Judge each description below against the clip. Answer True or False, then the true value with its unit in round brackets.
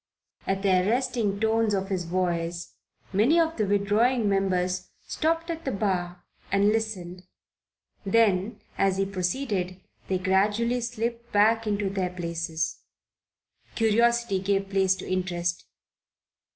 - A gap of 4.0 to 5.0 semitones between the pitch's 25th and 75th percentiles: False (3.6 semitones)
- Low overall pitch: False (195 Hz)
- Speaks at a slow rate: True (125 wpm)